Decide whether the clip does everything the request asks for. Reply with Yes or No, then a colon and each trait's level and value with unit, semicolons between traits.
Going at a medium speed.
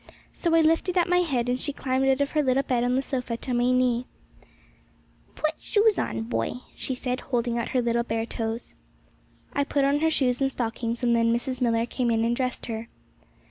No: fast, 220 wpm